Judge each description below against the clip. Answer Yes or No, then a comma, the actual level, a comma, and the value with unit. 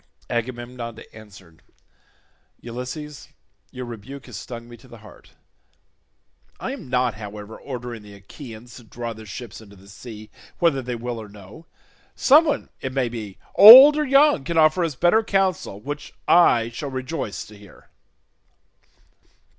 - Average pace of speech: Yes, average, 145 wpm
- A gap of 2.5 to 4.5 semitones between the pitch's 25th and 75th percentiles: No, average, 5.1 semitones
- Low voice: Yes, low, 120 Hz